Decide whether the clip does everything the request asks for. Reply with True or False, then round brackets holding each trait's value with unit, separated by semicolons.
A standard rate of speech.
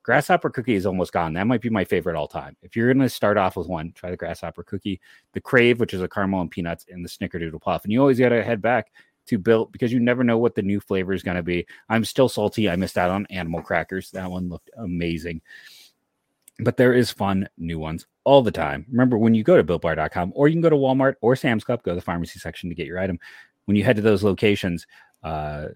False (250 wpm)